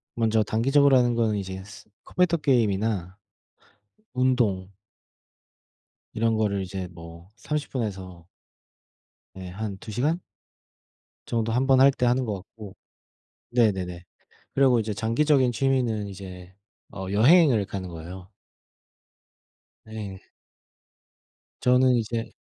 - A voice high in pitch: No, low, 110 Hz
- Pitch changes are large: No, average, 4.7 semitones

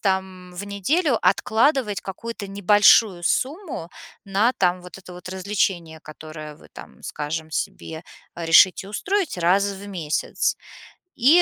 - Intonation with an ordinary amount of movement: Yes, average, 3.5 semitones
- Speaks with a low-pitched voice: No, high, 190 Hz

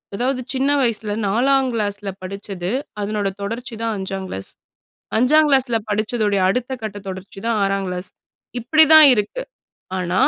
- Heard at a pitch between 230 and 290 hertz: No, high, 215 Hz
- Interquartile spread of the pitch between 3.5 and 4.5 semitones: Yes, average, 4.2 semitones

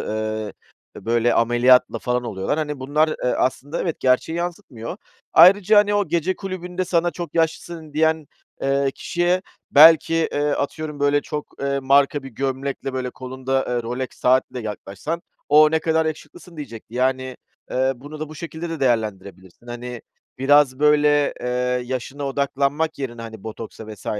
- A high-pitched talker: No, medium, 140 Hz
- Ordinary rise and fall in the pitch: Yes, average, 4.3 semitones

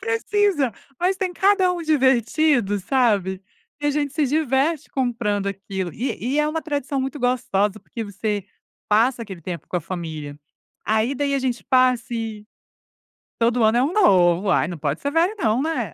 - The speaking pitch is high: Yes, high, 245 Hz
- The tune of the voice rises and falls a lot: Yes, wide, 6.4 semitones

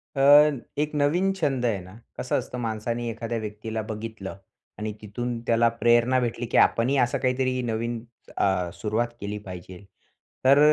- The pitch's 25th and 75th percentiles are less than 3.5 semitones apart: Yes, average, 2.7 semitones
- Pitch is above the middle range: No, low, 115 Hz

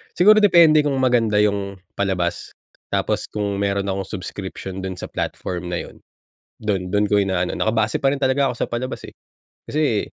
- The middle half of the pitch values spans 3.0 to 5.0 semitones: No, wide, 5.4 semitones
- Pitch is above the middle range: No, low, 105 Hz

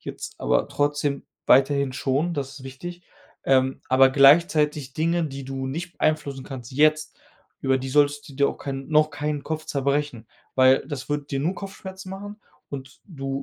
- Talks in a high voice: No, medium, 145 Hz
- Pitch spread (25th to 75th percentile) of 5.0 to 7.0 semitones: No, narrow, 2.4 semitones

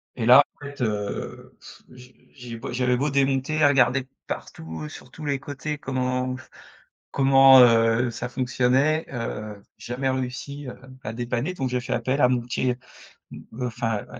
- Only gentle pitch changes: Yes, narrow, 2.0 semitones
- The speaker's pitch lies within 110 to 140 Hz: Yes, low, 125 Hz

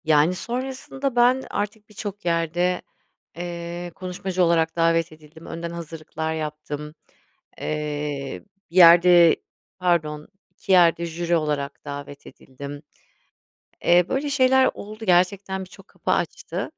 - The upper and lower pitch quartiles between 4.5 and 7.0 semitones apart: No, average, 3.5 semitones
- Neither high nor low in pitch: Yes, medium, 170 Hz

